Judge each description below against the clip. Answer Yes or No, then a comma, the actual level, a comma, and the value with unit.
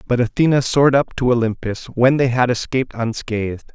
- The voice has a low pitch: Yes, low, 125 Hz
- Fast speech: No, average, 175 wpm